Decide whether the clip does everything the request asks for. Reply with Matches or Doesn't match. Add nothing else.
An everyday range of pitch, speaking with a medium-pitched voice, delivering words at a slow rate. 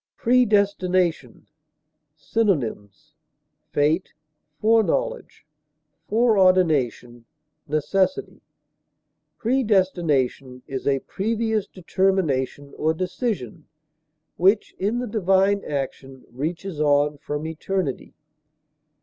Doesn't match